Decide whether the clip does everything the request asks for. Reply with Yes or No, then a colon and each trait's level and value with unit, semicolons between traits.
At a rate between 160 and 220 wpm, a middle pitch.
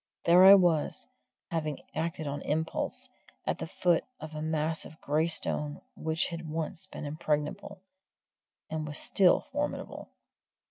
No: average, 140 wpm; medium, 160 Hz